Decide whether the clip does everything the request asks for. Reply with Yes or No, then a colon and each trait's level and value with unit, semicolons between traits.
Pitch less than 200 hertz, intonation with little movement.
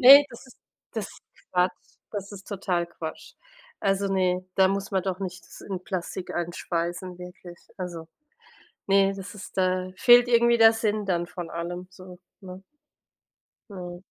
Yes: medium, 185 Hz; narrow, 1.9 semitones